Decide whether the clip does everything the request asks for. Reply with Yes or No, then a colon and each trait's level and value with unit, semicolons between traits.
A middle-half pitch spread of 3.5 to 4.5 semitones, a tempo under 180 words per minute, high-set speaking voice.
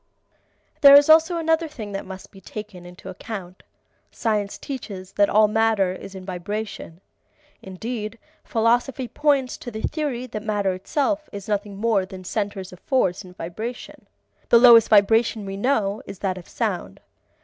Yes: average, 4.0 semitones; average, 160 wpm; high, 210 Hz